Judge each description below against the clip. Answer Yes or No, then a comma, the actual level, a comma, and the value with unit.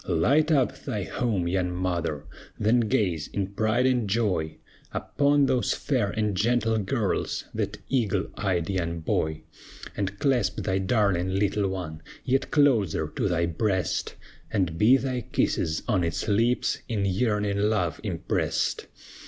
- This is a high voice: No, low, 100 Hz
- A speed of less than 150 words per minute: Yes, average, 140 wpm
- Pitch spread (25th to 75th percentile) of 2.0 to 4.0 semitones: No, average, 4.6 semitones